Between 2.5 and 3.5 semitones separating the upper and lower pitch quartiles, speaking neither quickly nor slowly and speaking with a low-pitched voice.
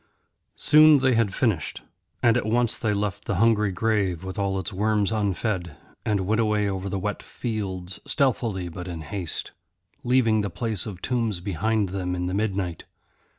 Yes: average, 3.2 semitones; average, 170 wpm; low, 105 Hz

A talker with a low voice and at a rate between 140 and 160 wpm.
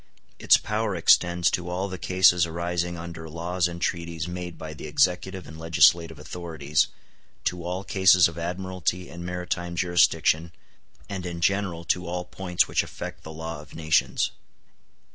Yes: very low, 85 Hz; average, 155 wpm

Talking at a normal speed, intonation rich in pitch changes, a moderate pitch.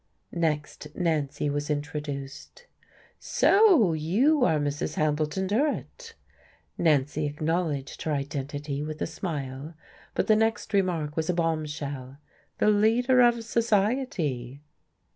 No: slow, 110 wpm; wide, 6.5 semitones; medium, 155 Hz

